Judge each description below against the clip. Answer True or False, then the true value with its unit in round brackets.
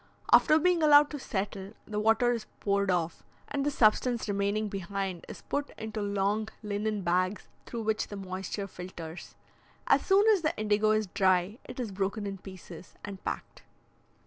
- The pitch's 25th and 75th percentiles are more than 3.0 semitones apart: False (2.6 semitones)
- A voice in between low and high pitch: False (205 Hz)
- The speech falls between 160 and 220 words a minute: True (170 wpm)